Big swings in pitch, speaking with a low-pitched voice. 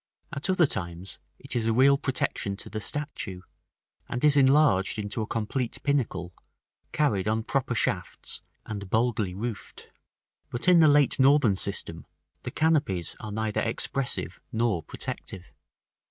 Yes: wide, 5.7 semitones; low, 115 Hz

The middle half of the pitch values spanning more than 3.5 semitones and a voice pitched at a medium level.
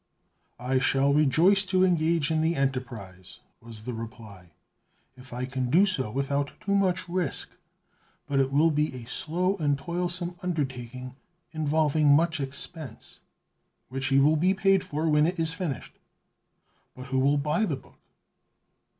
Yes: average, 4.5 semitones; medium, 145 Hz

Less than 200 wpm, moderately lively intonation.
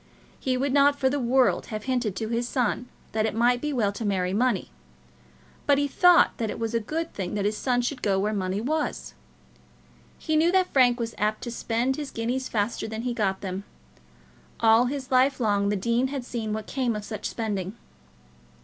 No: fast, 205 wpm; average, 3.8 semitones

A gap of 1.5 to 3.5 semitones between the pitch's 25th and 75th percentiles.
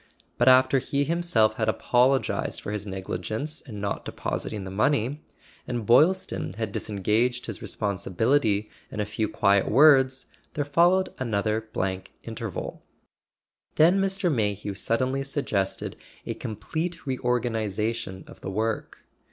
No: average, 5.1 semitones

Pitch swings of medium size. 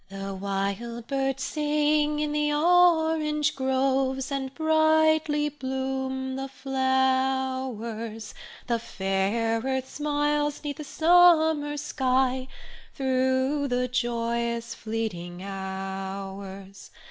Yes: average, 4.5 semitones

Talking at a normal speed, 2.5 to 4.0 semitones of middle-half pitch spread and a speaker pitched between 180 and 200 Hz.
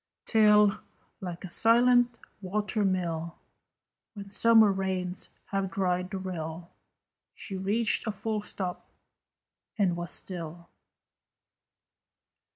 No: slow, 100 wpm; average, 2.9 semitones; high, 190 Hz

